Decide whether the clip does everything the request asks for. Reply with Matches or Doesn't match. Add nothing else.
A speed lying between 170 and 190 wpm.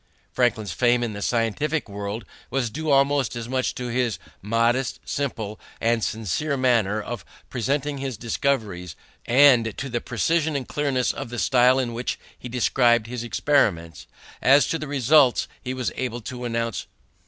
Doesn't match